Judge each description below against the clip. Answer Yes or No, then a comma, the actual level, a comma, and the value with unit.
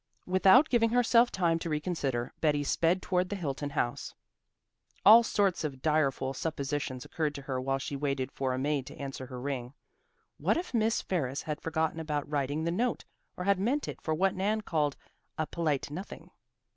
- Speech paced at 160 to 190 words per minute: Yes, average, 185 wpm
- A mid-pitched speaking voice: Yes, medium, 155 Hz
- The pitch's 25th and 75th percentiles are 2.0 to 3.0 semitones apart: No, average, 5.3 semitones